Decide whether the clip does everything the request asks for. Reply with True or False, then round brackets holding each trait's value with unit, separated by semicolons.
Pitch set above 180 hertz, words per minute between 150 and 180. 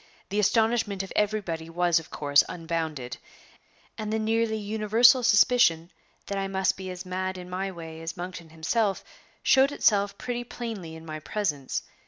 True (190 Hz; 160 wpm)